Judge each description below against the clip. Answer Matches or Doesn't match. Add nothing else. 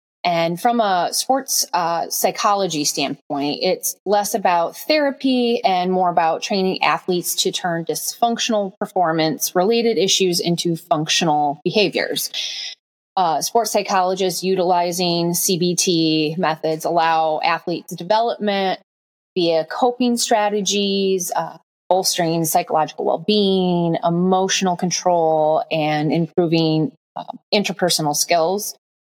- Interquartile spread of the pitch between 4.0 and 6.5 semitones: Doesn't match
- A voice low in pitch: Doesn't match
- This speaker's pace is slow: Matches